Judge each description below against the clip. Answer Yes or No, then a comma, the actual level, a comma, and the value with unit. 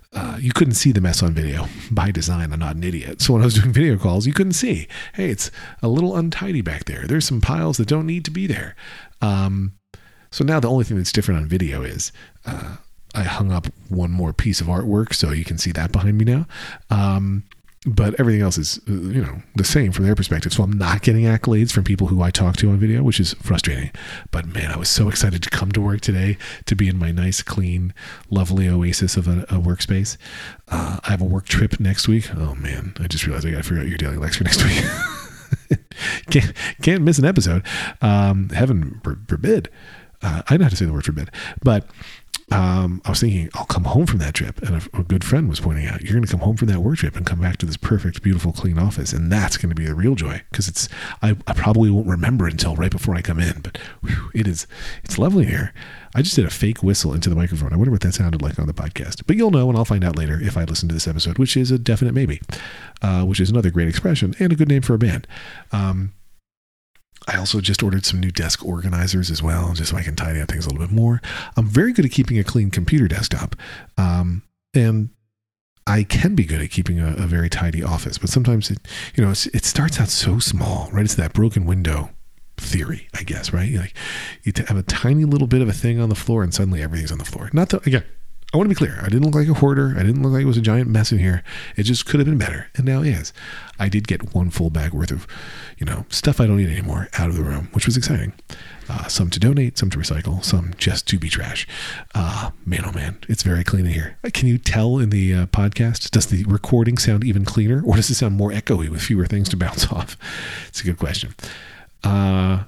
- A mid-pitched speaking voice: No, low, 100 Hz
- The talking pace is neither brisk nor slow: No, fast, 250 wpm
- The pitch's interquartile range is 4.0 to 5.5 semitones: Yes, average, 4.5 semitones